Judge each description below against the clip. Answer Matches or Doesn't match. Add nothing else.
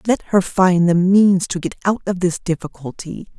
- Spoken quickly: Doesn't match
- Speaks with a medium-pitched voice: Matches